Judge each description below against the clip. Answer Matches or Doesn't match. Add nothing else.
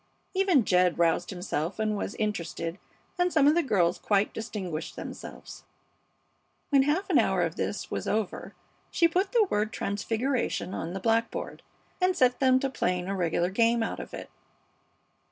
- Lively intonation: Matches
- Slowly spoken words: Doesn't match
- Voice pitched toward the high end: Matches